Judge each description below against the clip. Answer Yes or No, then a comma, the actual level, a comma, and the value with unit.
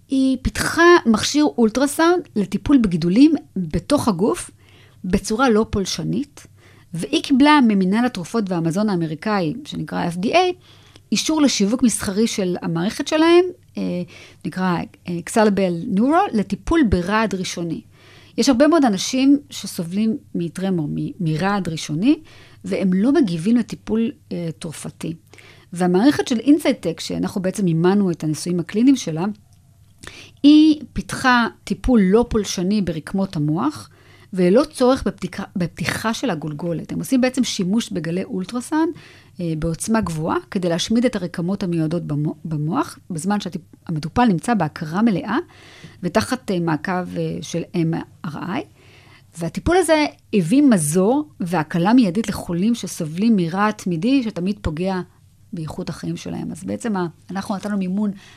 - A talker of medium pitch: No, high, 195 Hz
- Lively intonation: Yes, wide, 6.0 semitones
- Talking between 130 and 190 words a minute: No, average, 115 wpm